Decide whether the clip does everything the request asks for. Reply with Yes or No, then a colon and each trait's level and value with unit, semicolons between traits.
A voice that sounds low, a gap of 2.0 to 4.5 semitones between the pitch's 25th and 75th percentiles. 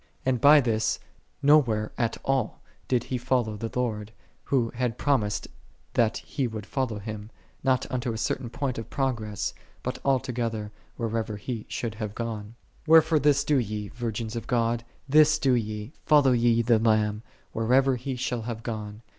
Yes: low, 115 Hz; average, 3.2 semitones